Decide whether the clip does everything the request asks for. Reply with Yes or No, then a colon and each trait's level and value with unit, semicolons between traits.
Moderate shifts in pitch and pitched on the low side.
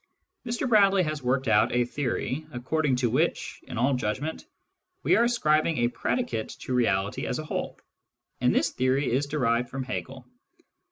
Yes: average, 4.0 semitones; low, 130 Hz